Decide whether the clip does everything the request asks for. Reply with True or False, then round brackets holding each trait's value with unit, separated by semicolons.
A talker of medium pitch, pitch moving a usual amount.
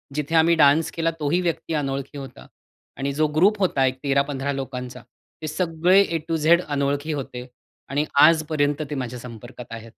True (145 Hz; 3.2 semitones)